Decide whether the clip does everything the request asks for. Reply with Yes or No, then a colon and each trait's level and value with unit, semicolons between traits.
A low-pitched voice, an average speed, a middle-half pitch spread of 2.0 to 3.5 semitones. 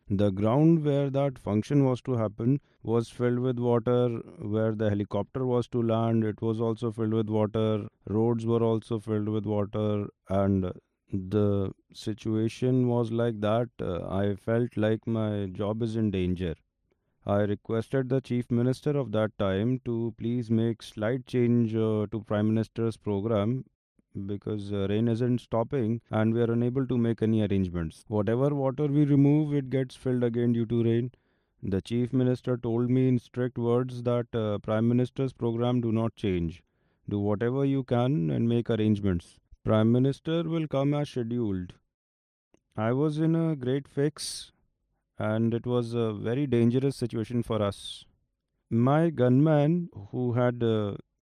Yes: low, 115 Hz; average, 160 wpm; average, 2.8 semitones